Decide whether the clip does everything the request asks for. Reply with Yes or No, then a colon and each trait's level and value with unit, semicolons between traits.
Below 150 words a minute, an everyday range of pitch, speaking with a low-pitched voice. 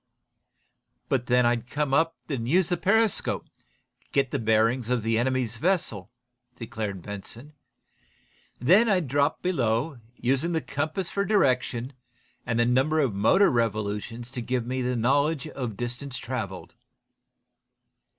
Yes: average, 140 wpm; average, 4.6 semitones; low, 125 Hz